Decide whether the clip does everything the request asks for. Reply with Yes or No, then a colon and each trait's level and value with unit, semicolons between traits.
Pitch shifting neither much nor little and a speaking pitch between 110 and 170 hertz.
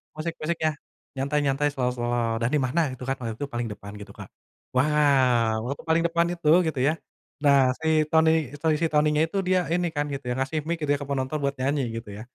Yes: average, 3.5 semitones; medium, 140 Hz